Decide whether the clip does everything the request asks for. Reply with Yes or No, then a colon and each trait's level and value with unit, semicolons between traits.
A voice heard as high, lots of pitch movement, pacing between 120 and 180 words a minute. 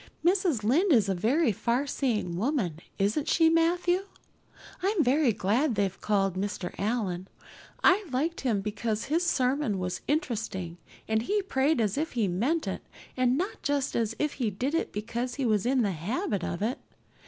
Yes: high, 240 Hz; wide, 6.7 semitones; average, 170 wpm